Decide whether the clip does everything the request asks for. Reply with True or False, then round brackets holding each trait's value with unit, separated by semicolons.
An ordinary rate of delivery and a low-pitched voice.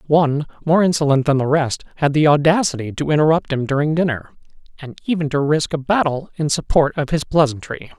False (190 wpm; 150 Hz)